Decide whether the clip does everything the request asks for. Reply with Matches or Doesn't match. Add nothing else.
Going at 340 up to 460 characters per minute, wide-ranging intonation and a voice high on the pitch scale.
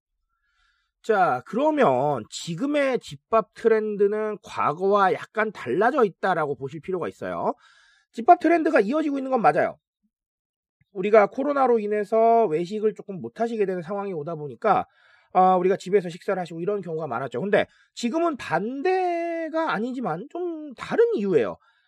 Doesn't match